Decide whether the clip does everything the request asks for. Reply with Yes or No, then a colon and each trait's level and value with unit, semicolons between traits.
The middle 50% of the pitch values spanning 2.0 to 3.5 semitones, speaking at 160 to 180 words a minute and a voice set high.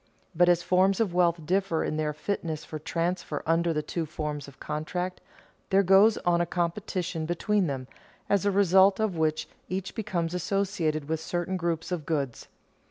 No: average, 3.2 semitones; average, 170 wpm; medium, 175 Hz